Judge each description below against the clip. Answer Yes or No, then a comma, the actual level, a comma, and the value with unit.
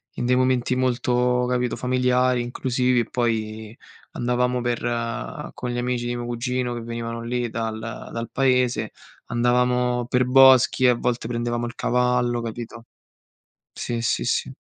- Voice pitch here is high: No, low, 120 Hz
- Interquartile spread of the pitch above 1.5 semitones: No, narrow, 1.0 semitones